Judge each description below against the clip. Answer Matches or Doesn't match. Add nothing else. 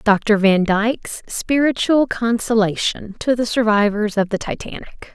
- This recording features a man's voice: Doesn't match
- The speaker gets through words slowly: Matches